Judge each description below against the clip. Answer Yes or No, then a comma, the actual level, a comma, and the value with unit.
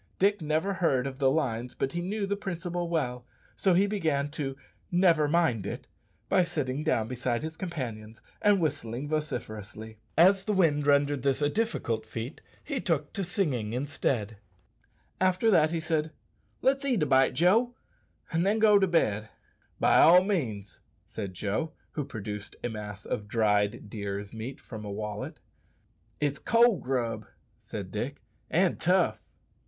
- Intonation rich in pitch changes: Yes, wide, 7.6 semitones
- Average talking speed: Yes, average, 160 wpm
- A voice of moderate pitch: Yes, medium, 145 Hz